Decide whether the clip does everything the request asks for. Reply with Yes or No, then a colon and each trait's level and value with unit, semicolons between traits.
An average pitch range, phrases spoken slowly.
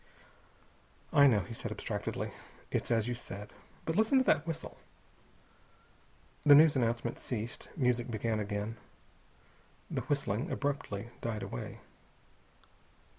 Yes: average, 4.8 semitones; slow, 120 wpm